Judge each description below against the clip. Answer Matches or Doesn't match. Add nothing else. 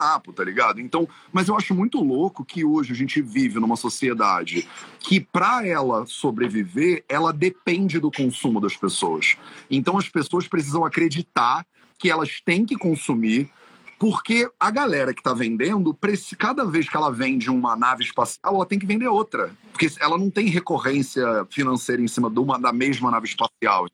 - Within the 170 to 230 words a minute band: Matches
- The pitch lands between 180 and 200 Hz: Doesn't match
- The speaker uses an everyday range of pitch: Doesn't match